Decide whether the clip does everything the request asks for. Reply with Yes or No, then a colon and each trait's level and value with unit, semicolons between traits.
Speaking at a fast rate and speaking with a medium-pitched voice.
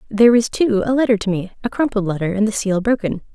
No: fast, 250 wpm; high, 215 Hz